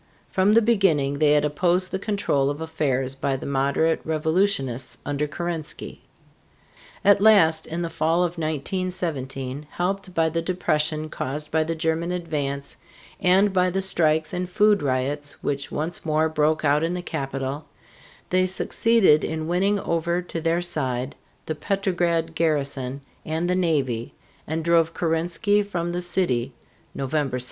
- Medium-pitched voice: Yes, medium, 160 Hz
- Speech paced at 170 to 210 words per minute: No, average, 150 wpm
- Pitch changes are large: No, average, 3.6 semitones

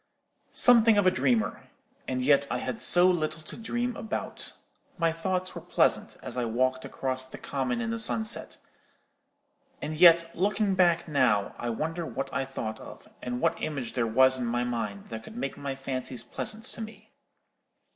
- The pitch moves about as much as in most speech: No, wide, 6.5 semitones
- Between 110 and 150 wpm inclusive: No, average, 175 wpm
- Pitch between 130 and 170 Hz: Yes, medium, 140 Hz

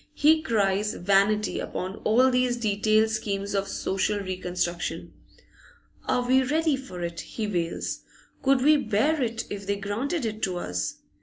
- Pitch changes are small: No, average, 4.5 semitones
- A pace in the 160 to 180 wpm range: No, average, 150 wpm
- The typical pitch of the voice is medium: No, high, 215 Hz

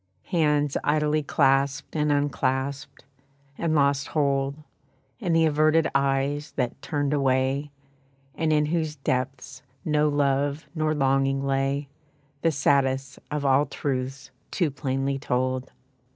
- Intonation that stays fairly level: Yes, narrow, 1.7 semitones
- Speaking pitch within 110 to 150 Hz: Yes, medium, 140 Hz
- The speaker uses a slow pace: Yes, slow, 120 wpm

